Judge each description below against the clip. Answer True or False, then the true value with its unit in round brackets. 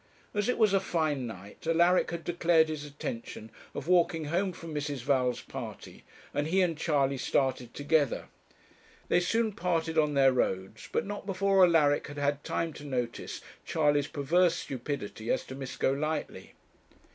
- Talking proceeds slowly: False (160 wpm)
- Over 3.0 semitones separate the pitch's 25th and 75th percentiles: True (4.1 semitones)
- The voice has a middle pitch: True (150 Hz)